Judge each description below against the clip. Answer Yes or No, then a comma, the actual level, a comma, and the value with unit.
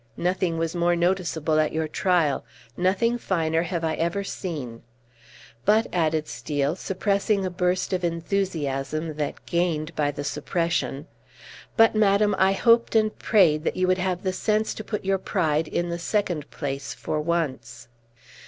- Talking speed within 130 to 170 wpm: Yes, average, 155 wpm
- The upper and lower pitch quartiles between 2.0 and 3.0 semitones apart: No, average, 3.7 semitones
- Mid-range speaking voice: Yes, medium, 170 Hz